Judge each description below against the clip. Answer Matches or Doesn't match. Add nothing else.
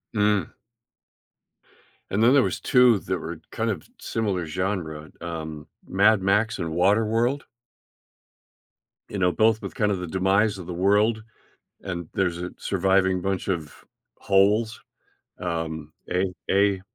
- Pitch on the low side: Matches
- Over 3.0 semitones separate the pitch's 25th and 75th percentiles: Matches